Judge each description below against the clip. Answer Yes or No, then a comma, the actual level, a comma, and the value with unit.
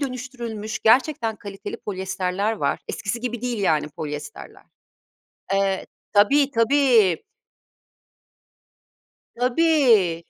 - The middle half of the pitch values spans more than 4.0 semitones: Yes, average, 4.7 semitones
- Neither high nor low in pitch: No, high, 220 Hz